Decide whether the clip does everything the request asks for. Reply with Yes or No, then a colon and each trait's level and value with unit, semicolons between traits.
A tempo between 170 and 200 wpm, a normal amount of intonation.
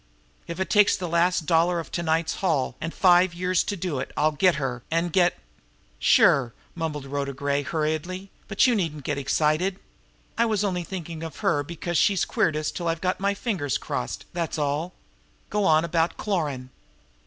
Yes: average, 190 wpm; average, 3.4 semitones